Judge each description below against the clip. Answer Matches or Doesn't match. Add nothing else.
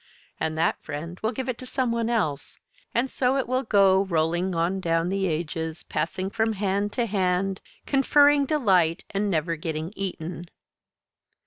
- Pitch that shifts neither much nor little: Doesn't match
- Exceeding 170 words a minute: Doesn't match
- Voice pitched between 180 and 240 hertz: Matches